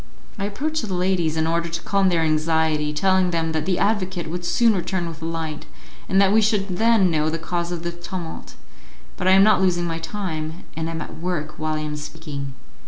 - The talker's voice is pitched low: No, medium, 170 Hz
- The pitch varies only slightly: No, average, 3.0 semitones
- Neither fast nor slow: No, fast, 220 wpm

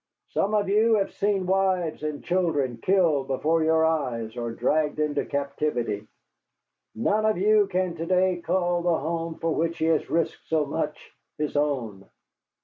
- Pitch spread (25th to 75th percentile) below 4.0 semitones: No, average, 4.3 semitones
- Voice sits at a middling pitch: Yes, medium, 160 Hz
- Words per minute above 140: Yes, average, 160 wpm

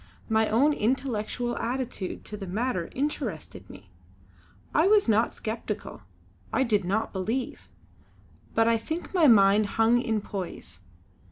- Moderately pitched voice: No, high, 225 Hz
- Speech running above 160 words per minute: No, slow, 135 wpm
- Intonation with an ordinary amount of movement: Yes, average, 4.1 semitones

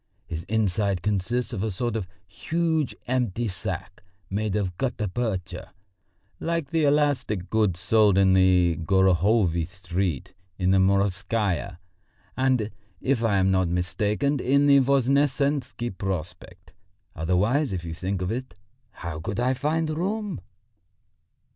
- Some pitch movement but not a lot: No, wide, 5.9 semitones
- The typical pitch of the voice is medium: No, low, 105 Hz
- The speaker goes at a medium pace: No, slow, 130 wpm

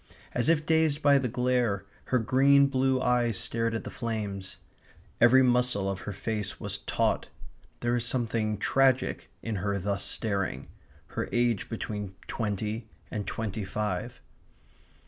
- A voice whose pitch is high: No, low, 115 Hz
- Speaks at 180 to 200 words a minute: No, average, 145 wpm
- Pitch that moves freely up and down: No, average, 3.6 semitones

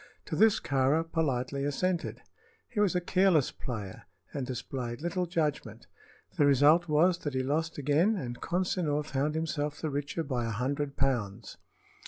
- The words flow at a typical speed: Yes, average, 155 wpm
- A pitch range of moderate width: Yes, average, 4.1 semitones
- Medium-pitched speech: Yes, medium, 145 Hz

